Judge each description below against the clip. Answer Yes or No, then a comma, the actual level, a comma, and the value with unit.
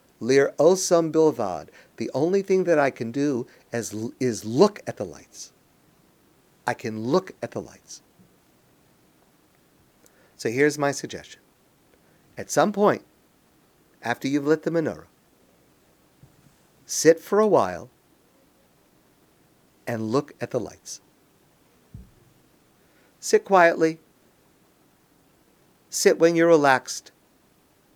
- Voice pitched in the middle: Yes, medium, 145 Hz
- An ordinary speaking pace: No, slow, 105 wpm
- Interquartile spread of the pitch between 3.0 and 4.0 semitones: No, average, 5.2 semitones